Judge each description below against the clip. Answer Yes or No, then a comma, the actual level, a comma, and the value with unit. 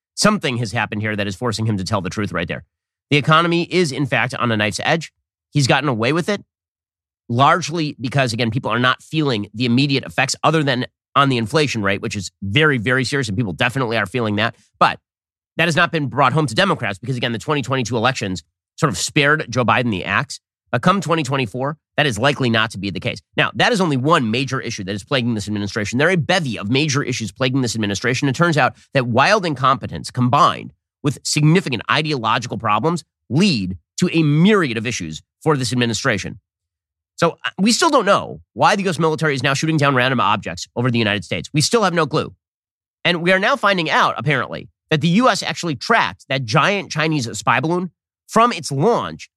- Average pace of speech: No, fast, 210 wpm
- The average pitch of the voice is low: Yes, low, 130 Hz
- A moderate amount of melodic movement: No, wide, 6.1 semitones